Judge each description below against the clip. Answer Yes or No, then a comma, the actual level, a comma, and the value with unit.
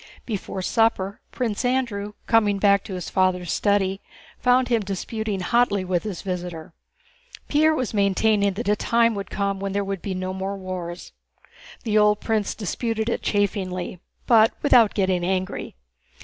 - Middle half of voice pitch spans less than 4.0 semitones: Yes, average, 2.9 semitones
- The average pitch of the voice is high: Yes, high, 200 Hz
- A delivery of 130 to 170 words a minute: Yes, average, 155 wpm